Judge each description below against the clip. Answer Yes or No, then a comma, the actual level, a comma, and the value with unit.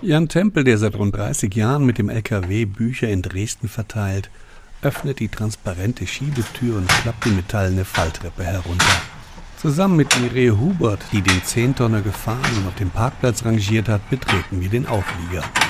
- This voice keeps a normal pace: Yes, average, 160 wpm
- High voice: No, low, 110 Hz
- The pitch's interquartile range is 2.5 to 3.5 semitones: No, average, 4.1 semitones